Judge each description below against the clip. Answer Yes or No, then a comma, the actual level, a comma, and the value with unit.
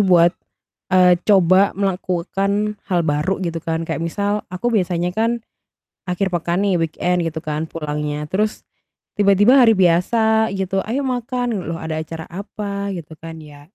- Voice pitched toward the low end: No, medium, 185 Hz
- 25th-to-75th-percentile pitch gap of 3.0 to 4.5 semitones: Yes, average, 3.6 semitones